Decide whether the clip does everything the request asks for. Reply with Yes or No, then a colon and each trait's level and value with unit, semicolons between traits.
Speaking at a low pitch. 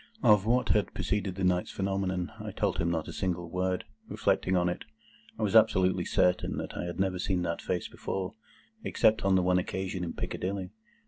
Yes: very low, 95 Hz